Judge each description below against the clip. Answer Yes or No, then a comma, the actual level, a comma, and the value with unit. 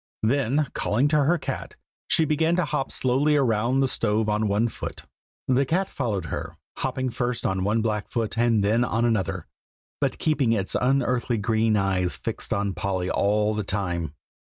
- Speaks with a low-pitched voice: Yes, low, 115 Hz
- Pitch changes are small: No, average, 4.4 semitones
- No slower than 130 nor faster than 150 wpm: No, average, 175 wpm